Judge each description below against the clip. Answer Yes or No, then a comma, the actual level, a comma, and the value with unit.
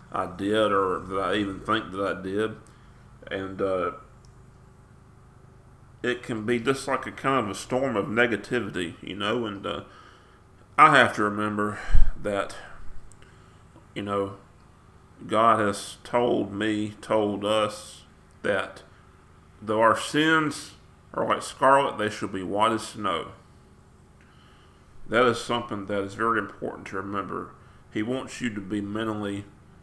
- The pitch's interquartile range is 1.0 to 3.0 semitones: No, average, 3.9 semitones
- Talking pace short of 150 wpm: Yes, average, 140 wpm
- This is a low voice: Yes, low, 105 Hz